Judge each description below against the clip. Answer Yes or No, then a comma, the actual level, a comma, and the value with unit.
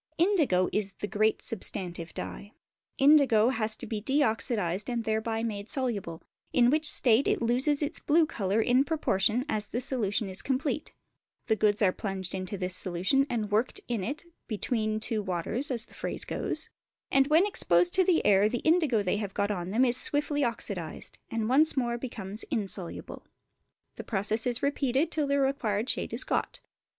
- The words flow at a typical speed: Yes, average, 180 wpm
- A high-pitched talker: Yes, high, 225 Hz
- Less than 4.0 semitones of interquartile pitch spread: No, average, 4.9 semitones